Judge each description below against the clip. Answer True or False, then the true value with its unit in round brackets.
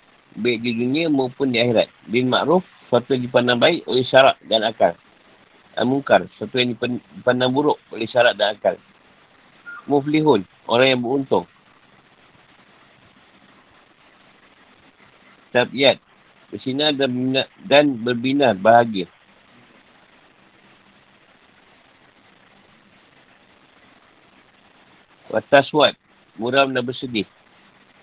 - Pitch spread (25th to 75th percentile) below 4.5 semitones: False (4.9 semitones)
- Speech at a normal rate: False (85 wpm)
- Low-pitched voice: True (125 Hz)